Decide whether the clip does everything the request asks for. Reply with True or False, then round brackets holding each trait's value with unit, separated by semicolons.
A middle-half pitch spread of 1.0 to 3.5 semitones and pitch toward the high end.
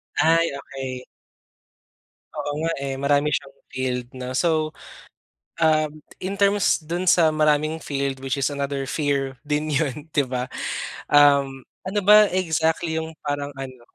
False (2.9 semitones; 145 Hz)